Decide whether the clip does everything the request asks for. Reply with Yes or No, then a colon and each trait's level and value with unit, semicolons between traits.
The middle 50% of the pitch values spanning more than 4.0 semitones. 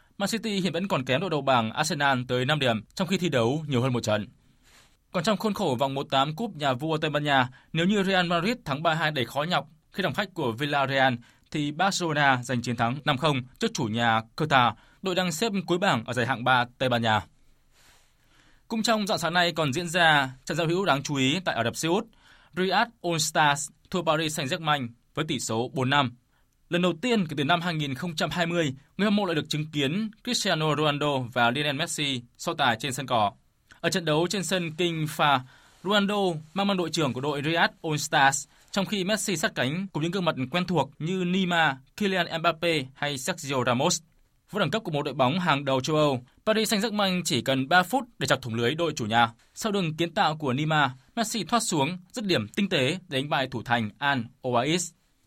Yes: wide, 5.4 semitones